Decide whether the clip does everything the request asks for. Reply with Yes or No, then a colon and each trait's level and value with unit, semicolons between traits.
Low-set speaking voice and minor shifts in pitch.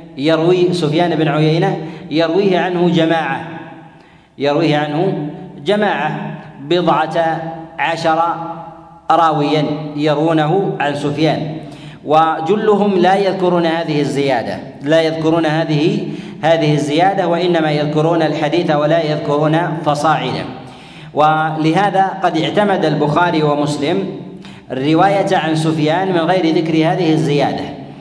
No: medium, 160 Hz; narrow, 2.2 semitones